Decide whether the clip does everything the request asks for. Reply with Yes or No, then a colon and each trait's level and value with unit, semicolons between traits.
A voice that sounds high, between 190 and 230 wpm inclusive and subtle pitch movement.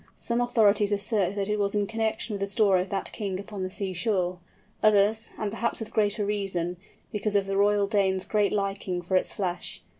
Yes: high, 200 Hz; average, 200 wpm; narrow, 1.7 semitones